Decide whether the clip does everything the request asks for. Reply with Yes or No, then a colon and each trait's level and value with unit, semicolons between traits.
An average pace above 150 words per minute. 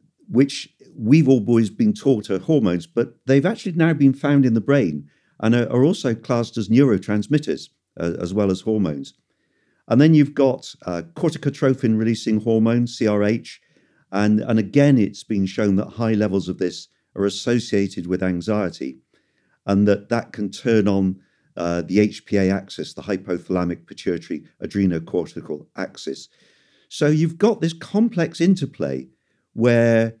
No: average, 145 wpm